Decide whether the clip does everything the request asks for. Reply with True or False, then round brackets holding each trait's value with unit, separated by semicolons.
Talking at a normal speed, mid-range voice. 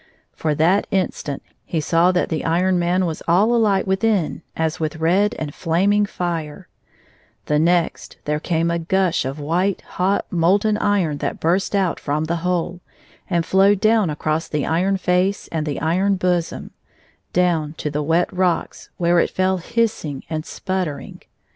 True (165 wpm; 175 Hz)